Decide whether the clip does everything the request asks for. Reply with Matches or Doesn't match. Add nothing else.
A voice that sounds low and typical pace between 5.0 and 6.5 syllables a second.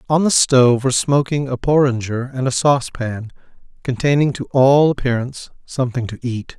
Matches